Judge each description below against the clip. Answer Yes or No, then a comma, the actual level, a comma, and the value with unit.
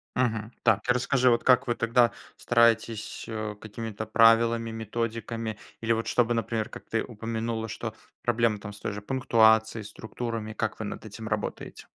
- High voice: No, low, 115 Hz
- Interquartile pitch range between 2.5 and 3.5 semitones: No, narrow, 1.2 semitones